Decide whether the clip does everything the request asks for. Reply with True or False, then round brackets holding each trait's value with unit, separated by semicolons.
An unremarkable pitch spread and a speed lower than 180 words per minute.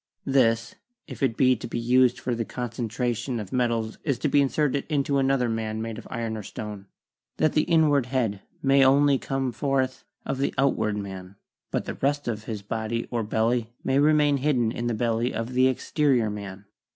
False (3.4 semitones; 190 wpm)